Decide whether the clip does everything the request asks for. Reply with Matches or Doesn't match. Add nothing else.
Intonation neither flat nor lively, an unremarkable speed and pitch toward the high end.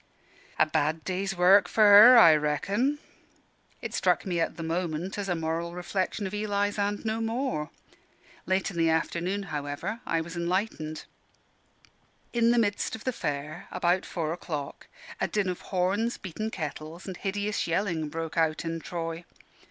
Doesn't match